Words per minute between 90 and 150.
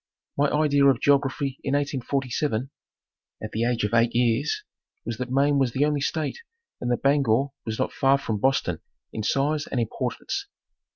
No: average, 170 wpm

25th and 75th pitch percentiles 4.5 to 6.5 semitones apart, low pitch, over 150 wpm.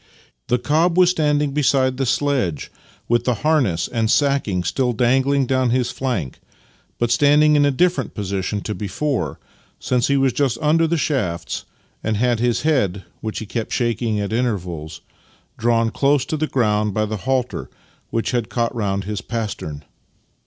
Yes: average, 4.9 semitones; low, 120 Hz; average, 165 wpm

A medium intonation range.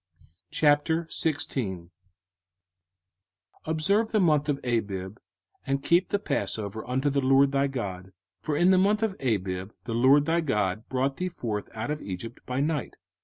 No: wide, 6.3 semitones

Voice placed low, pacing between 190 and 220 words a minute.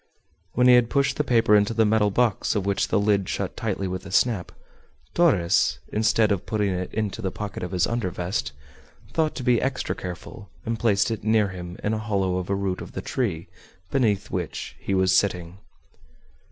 Yes: low, 105 Hz; average, 200 wpm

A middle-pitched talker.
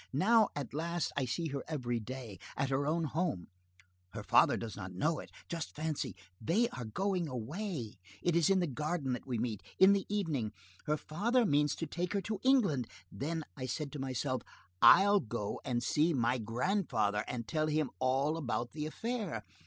Yes: medium, 150 Hz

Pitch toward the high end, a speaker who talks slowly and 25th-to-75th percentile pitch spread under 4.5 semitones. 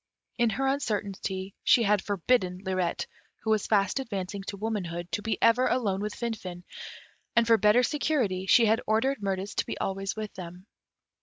No: high, 205 Hz; average, 170 wpm; average, 3.4 semitones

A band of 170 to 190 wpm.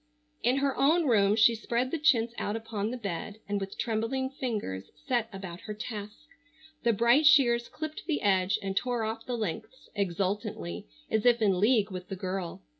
Yes: average, 185 wpm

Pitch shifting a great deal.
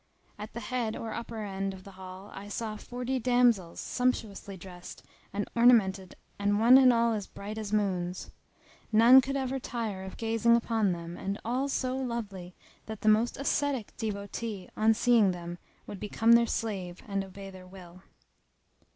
No: average, 3.5 semitones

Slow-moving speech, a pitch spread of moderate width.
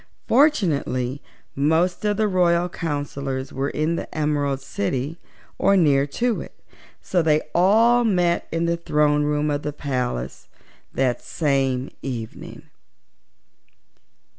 Yes: slow, 120 wpm; average, 4.3 semitones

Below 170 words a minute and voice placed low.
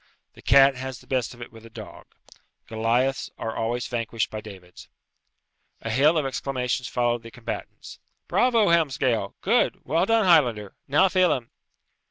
Yes: average, 155 wpm; low, 125 Hz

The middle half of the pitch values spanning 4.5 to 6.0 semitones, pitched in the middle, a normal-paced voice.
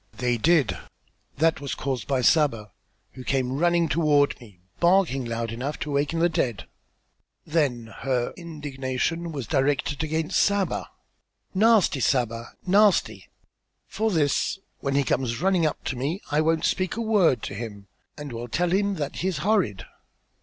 Yes: average, 5.2 semitones; medium, 145 Hz; average, 155 wpm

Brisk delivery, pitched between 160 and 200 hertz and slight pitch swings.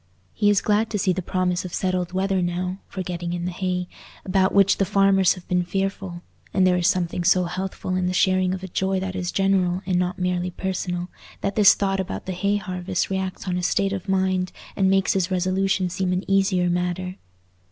Yes: fast, 215 wpm; medium, 185 Hz; narrow, 1.2 semitones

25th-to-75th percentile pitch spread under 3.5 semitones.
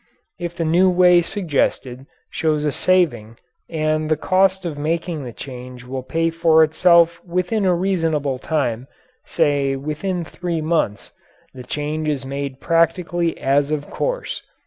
No: average, 3.8 semitones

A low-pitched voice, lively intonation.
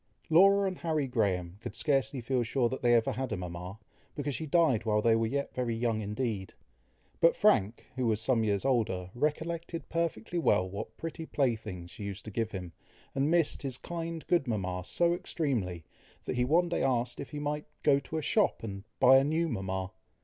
Yes: low, 125 Hz; wide, 6.5 semitones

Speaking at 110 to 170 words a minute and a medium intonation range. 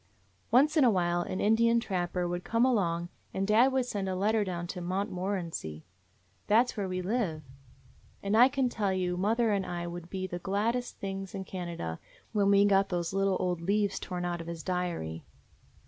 No: average, 195 wpm; average, 3.3 semitones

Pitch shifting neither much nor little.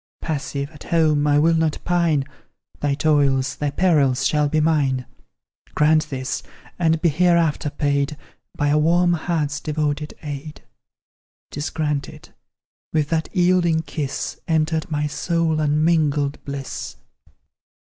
No: narrow, 2.0 semitones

